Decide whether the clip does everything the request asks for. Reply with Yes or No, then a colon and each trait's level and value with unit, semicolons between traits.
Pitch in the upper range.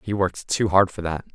No: very low, 95 Hz